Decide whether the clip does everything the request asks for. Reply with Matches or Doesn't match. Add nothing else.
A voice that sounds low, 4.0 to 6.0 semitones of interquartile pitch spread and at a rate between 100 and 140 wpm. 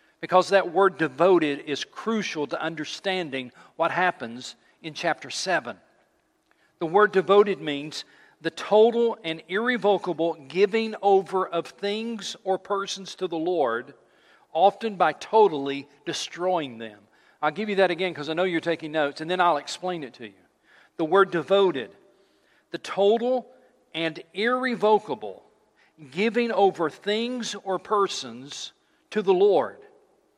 Doesn't match